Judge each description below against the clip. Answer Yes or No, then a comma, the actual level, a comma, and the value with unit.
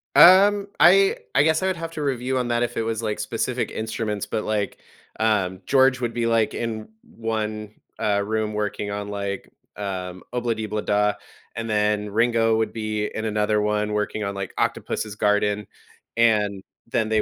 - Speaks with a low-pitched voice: Yes, low, 110 Hz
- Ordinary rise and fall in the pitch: No, narrow, 2.1 semitones